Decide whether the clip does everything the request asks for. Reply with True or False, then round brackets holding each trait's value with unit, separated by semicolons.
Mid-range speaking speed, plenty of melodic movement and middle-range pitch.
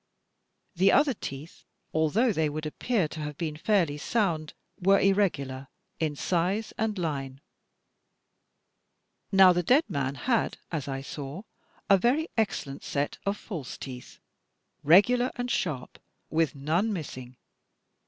False (130 wpm; 6.1 semitones; 165 Hz)